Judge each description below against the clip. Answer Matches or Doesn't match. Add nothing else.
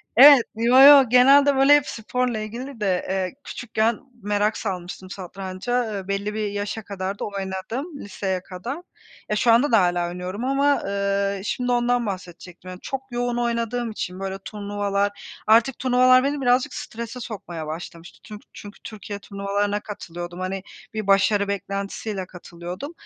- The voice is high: Matches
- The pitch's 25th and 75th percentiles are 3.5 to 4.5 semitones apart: Matches